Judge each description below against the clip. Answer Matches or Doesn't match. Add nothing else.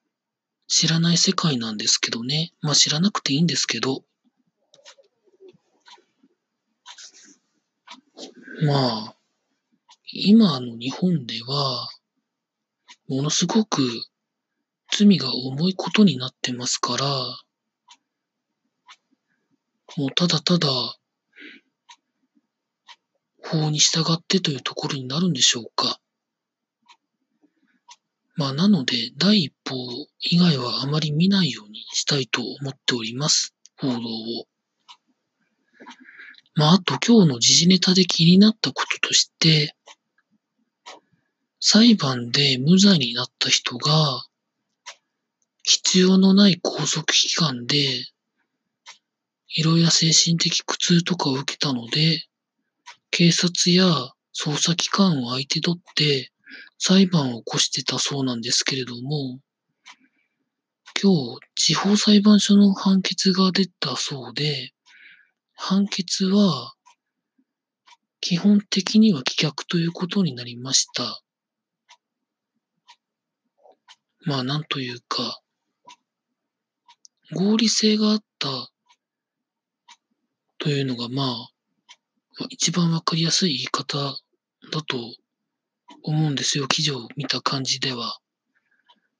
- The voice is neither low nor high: Matches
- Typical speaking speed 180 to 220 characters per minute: Matches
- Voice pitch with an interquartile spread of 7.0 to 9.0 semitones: Matches